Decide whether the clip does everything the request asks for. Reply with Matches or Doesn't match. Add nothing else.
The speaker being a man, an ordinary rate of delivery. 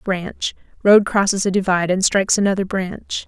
Doesn't match